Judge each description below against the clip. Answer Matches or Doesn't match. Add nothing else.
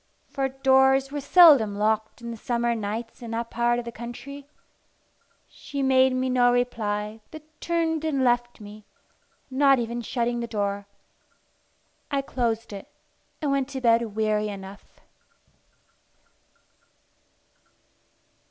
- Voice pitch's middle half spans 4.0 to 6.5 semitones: Doesn't match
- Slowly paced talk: Matches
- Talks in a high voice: Matches